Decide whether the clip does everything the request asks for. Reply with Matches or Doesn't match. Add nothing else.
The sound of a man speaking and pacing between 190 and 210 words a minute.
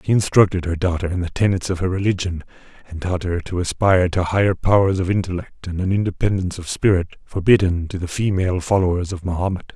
Matches